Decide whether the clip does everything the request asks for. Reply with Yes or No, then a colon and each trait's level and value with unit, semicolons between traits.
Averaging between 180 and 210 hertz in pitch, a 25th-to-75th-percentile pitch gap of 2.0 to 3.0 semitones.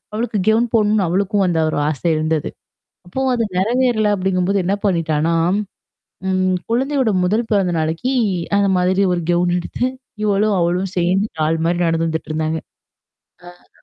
No: medium, 185 Hz; average, 4.1 semitones